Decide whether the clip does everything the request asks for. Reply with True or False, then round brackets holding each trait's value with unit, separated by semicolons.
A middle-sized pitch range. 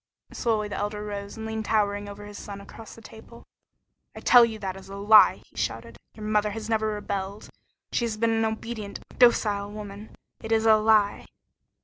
False (1.5 semitones)